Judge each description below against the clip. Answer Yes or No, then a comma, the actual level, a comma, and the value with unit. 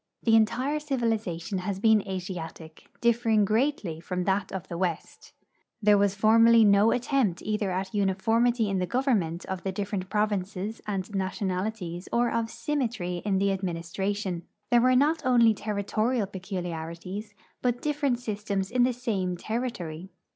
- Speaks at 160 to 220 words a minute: No, average, 145 wpm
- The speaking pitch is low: No, high, 205 Hz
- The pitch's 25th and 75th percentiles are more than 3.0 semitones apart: Yes, average, 3.8 semitones